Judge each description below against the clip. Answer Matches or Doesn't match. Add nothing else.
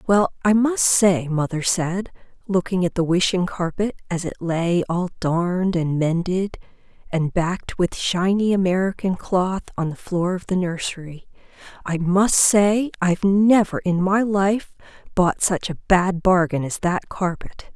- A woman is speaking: Matches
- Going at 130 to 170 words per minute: Matches